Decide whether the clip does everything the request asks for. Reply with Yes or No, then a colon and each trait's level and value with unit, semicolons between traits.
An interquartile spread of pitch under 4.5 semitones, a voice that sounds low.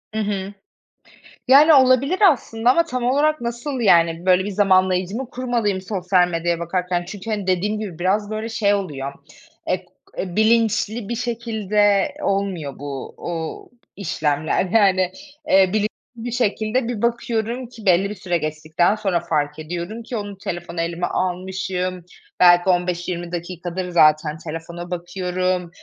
No: average, 4.0 semitones; high, 190 Hz